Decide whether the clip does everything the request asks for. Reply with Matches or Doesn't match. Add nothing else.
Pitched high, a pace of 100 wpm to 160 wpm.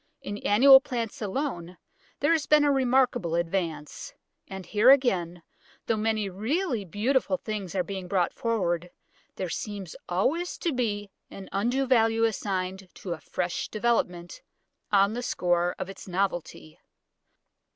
Matches